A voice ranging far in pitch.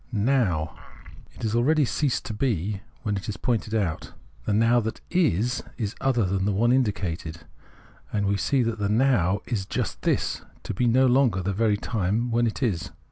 No: average, 3.7 semitones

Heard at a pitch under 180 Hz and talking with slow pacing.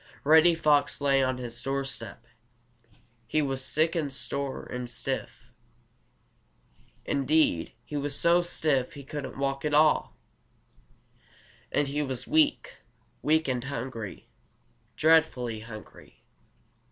Yes: medium, 140 Hz; slow, 115 wpm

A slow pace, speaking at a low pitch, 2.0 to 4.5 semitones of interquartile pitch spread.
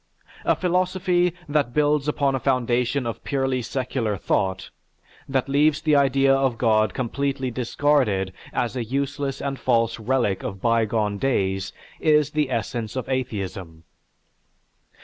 Yes: slow, 130 wpm; low, 130 Hz; average, 3.8 semitones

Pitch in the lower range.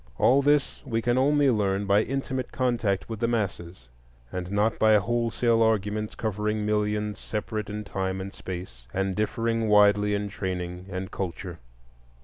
Yes: low, 105 Hz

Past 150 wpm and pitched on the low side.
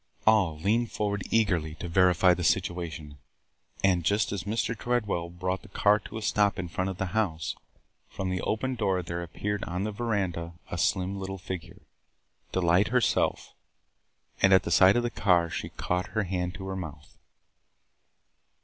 Yes: average, 175 wpm; very low, 95 Hz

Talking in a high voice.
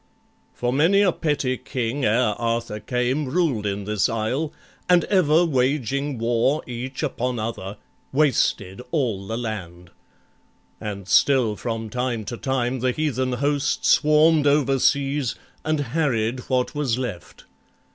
No: low, 125 Hz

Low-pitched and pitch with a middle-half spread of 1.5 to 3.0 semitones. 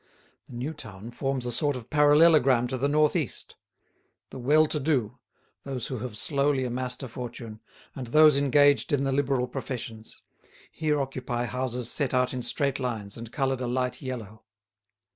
Yes: low, 130 Hz; average, 2.7 semitones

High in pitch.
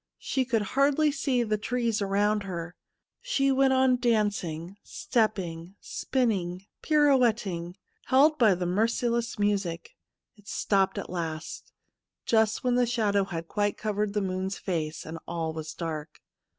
Yes: high, 205 Hz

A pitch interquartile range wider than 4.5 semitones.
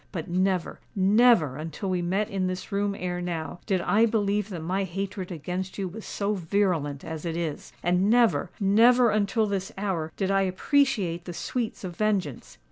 No: average, 2.9 semitones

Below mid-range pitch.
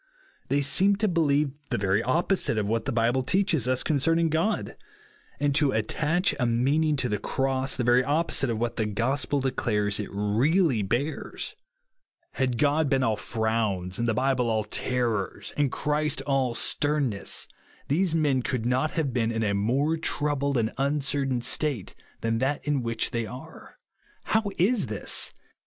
Yes: low, 130 Hz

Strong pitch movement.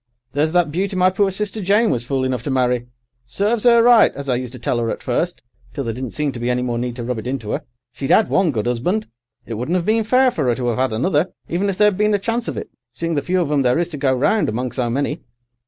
Yes: wide, 7.6 semitones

